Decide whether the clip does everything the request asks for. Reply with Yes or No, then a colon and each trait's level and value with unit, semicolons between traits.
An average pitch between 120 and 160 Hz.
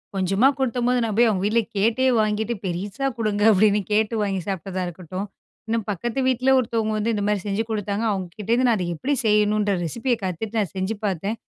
No: high, 210 Hz